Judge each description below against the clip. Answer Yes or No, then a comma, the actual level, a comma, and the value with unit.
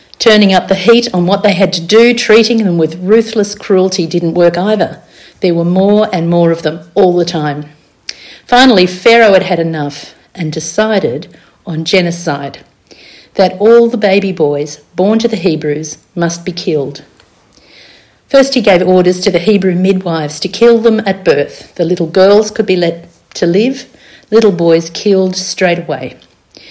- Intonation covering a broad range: No, average, 4.0 semitones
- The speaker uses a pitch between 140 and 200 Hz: Yes, medium, 185 Hz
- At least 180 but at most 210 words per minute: No, average, 170 wpm